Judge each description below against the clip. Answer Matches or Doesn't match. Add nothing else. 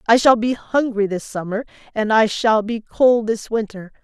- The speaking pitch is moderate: Doesn't match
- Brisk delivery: Doesn't match